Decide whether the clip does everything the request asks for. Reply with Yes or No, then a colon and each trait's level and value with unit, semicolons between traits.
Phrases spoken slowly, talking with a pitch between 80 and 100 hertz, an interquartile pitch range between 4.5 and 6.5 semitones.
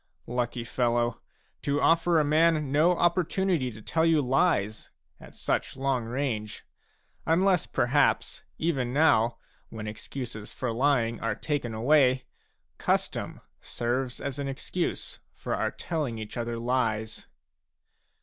No: slow, 125 wpm; low, 130 Hz; average, 4.8 semitones